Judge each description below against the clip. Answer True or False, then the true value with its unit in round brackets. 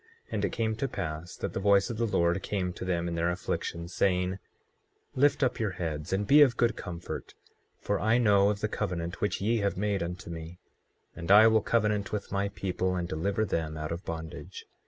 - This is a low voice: True (95 Hz)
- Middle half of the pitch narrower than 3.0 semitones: False (3.6 semitones)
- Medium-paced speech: False (215 wpm)